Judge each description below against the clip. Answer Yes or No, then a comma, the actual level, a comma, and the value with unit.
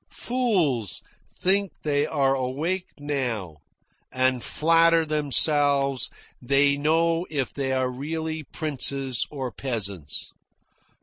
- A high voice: No, medium, 140 Hz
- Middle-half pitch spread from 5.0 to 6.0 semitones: No, average, 3.6 semitones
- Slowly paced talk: Yes, slow, 100 wpm